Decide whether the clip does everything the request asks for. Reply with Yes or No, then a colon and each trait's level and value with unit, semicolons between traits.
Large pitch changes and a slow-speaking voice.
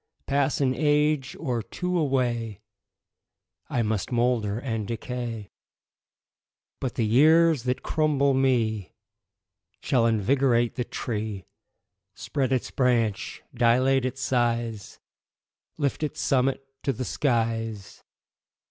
No: average, 3.0 semitones; slow, 105 wpm